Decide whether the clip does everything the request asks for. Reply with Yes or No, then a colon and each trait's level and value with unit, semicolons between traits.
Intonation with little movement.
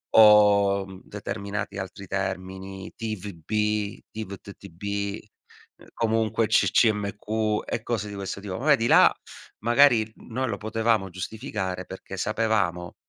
Yes: narrow, 2.3 semitones